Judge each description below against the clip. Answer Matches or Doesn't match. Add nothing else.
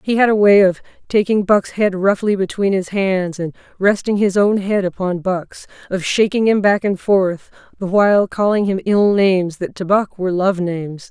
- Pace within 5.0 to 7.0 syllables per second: Doesn't match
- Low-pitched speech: Doesn't match